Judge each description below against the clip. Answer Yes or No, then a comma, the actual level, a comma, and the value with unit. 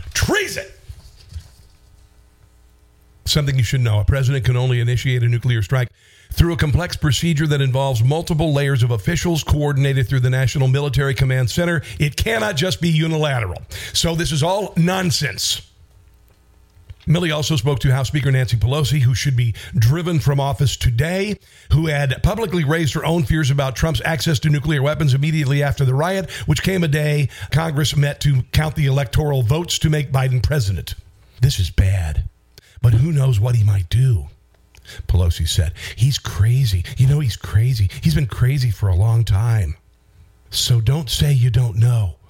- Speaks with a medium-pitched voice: No, low, 130 Hz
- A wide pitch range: Yes, wide, 6.3 semitones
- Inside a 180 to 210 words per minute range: No, average, 165 wpm